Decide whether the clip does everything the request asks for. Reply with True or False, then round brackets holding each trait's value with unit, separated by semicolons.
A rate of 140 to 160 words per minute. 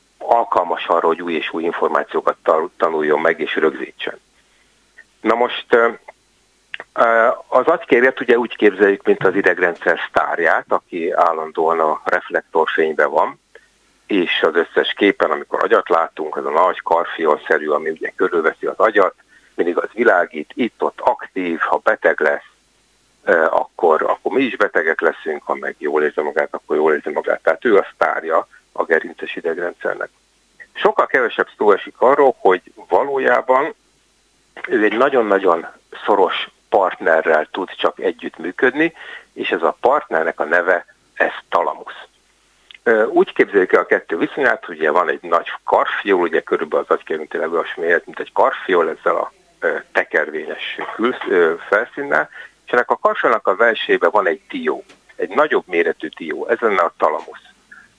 True (145 wpm)